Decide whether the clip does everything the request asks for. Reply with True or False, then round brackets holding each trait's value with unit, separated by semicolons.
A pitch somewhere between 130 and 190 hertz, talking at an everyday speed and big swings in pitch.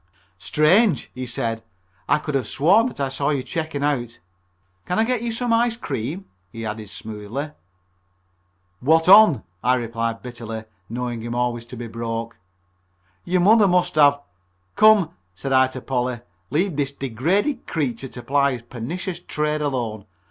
True (135 Hz; 160 wpm; 6.7 semitones)